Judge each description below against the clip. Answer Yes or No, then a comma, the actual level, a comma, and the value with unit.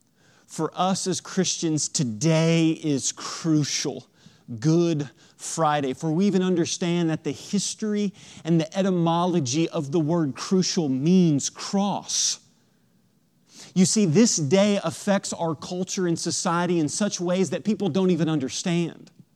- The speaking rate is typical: No, slow, 130 wpm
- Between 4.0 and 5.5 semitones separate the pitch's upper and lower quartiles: No, average, 2.9 semitones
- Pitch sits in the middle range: Yes, medium, 170 Hz